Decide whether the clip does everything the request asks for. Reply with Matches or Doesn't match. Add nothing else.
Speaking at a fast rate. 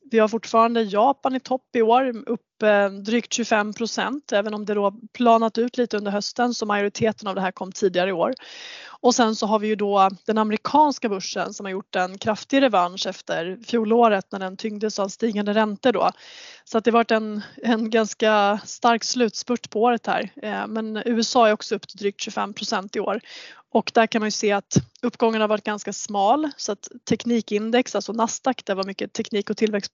Matches